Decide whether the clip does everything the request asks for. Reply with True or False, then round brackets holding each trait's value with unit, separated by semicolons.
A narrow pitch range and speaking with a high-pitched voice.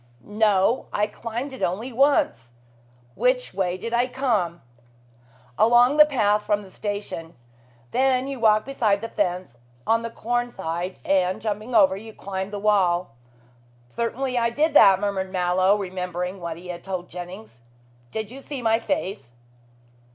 False (4.4 semitones; 205 Hz)